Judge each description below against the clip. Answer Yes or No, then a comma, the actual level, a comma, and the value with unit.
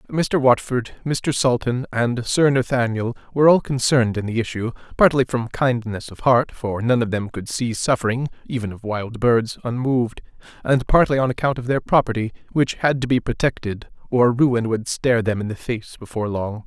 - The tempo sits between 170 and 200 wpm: Yes, average, 180 wpm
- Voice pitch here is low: Yes, low, 120 Hz